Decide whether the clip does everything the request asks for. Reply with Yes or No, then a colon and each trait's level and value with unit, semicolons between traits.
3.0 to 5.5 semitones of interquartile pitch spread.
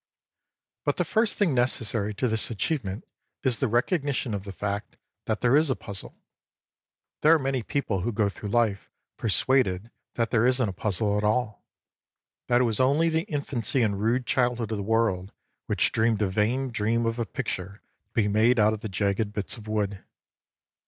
Yes: average, 3.6 semitones